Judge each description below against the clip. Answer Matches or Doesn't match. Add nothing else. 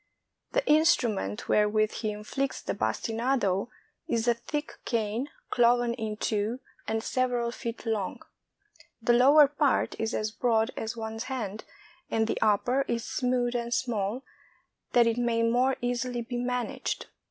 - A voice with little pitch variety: Matches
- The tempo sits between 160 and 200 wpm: Doesn't match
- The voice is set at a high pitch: Matches